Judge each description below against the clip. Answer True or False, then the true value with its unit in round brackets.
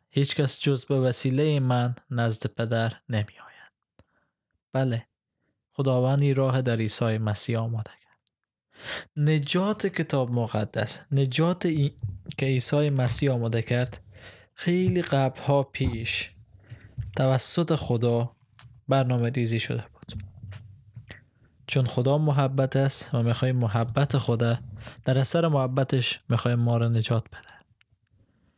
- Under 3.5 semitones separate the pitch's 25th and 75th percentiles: True (3.1 semitones)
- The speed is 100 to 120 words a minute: True (115 wpm)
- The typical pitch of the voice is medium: False (125 Hz)